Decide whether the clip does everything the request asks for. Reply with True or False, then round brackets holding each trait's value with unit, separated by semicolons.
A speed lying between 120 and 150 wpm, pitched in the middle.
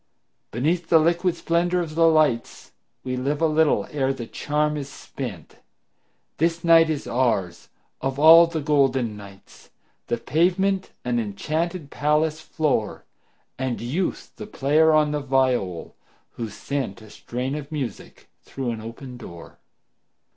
True (140 wpm; 145 Hz)